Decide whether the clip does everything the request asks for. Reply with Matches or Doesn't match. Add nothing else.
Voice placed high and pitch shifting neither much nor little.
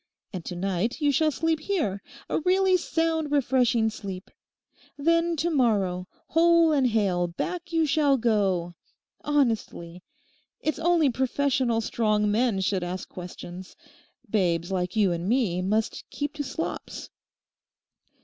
Doesn't match